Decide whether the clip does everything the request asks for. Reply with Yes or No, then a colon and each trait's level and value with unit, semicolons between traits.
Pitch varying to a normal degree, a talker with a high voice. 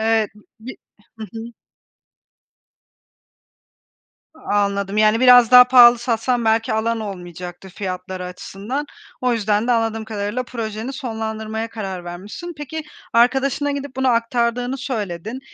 Yes: average, 3.3 semitones; high, 225 Hz